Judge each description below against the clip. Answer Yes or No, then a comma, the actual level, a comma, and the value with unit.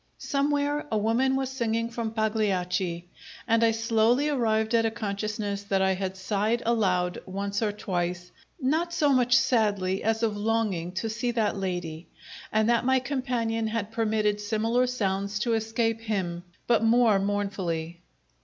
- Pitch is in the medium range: No, high, 220 Hz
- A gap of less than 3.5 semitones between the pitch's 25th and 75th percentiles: Yes, average, 2.9 semitones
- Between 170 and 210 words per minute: No, average, 155 wpm